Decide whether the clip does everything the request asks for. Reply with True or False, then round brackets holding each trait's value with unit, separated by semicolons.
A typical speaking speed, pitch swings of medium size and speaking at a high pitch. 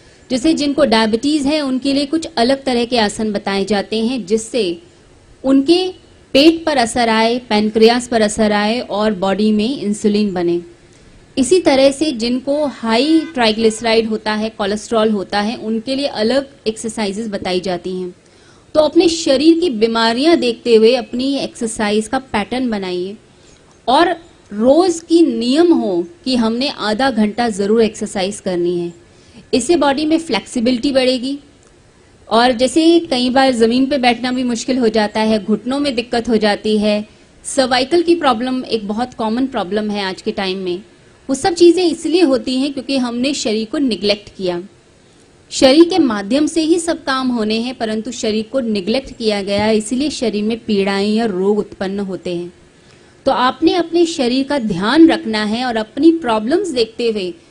True (165 wpm; 4.4 semitones; 235 Hz)